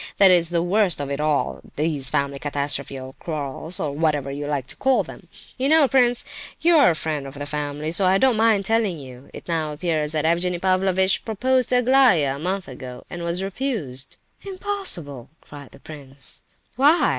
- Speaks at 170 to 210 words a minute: Yes, average, 190 wpm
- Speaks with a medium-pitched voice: Yes, medium, 165 Hz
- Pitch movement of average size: No, wide, 7.1 semitones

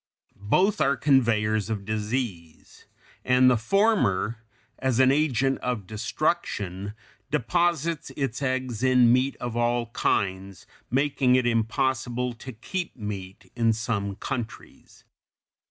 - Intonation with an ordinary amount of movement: Yes, average, 3.6 semitones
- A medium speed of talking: No, slow, 115 wpm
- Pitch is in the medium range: No, low, 120 Hz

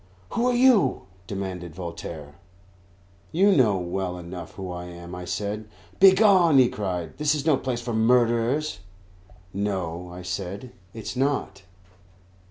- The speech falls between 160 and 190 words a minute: No, average, 140 wpm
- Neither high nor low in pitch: No, low, 105 Hz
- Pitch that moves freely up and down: Yes, wide, 7.4 semitones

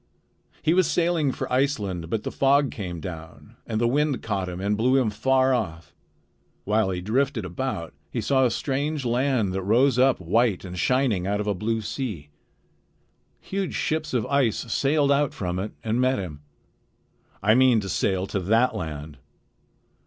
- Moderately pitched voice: No, low, 115 Hz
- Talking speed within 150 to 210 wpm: Yes, average, 175 wpm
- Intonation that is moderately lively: No, wide, 5.9 semitones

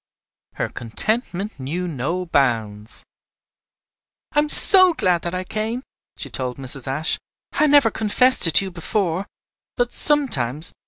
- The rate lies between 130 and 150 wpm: Yes, average, 140 wpm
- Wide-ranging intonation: Yes, wide, 9.0 semitones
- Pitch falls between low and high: Yes, medium, 180 Hz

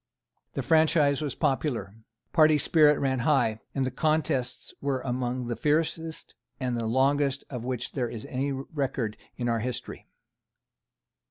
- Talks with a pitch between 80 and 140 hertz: Yes, low, 135 Hz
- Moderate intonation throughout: Yes, average, 3.3 semitones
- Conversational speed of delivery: Yes, average, 145 wpm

